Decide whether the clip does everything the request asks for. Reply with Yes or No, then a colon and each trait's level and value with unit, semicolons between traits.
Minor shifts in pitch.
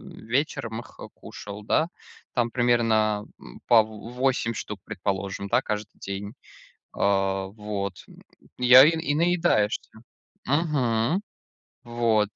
No: average, 3.4 semitones